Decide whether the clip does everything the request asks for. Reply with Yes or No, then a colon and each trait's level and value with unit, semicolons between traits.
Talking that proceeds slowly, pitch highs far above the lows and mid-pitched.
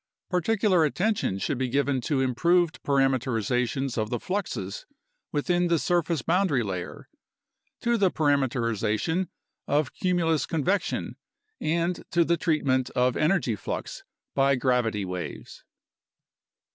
Yes: slow, 115 wpm; wide, 5.7 semitones; medium, 145 Hz